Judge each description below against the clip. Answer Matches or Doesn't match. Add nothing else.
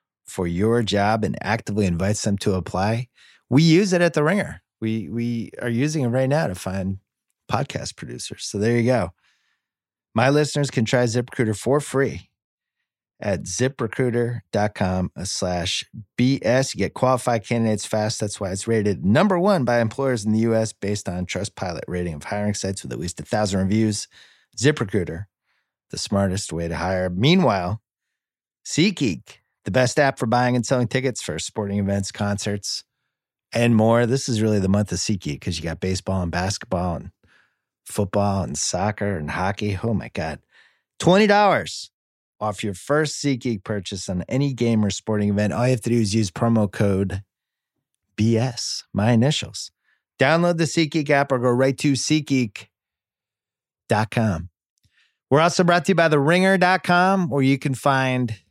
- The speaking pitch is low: Matches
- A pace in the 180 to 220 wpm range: Doesn't match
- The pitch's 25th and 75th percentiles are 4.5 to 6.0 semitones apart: Matches